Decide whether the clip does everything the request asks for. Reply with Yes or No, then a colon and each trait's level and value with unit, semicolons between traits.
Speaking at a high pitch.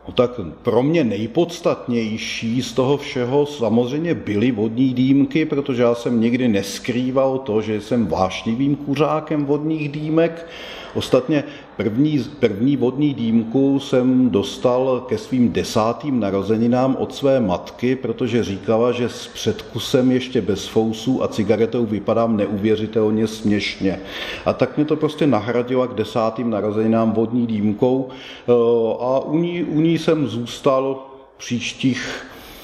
No: low, 125 Hz